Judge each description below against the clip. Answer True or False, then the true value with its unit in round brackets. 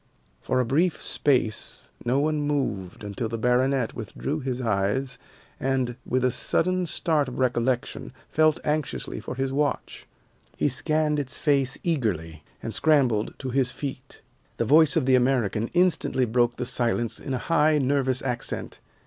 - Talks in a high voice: False (130 Hz)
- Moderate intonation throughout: True (3.4 semitones)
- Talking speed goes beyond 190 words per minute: False (155 wpm)